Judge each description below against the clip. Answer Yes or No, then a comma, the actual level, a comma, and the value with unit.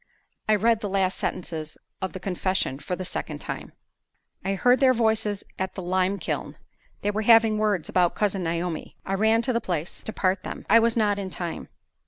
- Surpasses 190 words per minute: Yes, average, 200 wpm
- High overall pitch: Yes, high, 195 Hz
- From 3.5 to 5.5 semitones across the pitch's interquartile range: No, average, 3.1 semitones